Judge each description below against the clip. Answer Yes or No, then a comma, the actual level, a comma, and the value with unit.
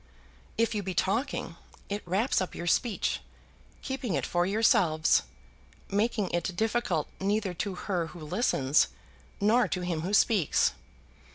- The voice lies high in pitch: Yes, high, 195 Hz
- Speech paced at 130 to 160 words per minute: Yes, slow, 135 wpm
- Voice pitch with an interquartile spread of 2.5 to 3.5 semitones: No, average, 4.0 semitones